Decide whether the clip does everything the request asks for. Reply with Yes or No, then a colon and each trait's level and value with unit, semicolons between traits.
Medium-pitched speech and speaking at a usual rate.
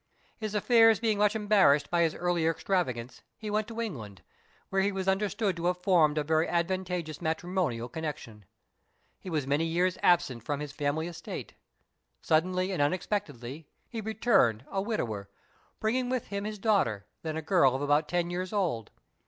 Yes: medium, 175 Hz; average, 170 wpm